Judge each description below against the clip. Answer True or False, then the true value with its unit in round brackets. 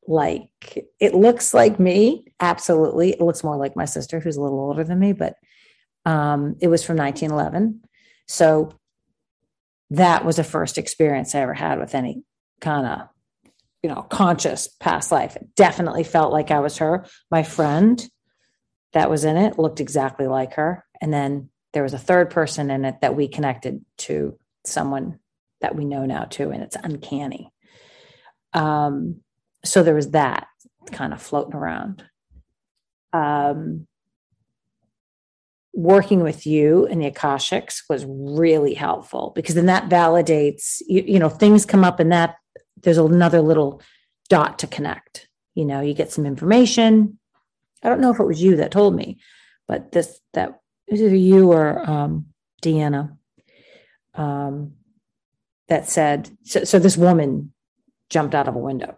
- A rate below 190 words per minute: True (160 wpm)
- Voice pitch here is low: False (160 Hz)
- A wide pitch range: False (3.9 semitones)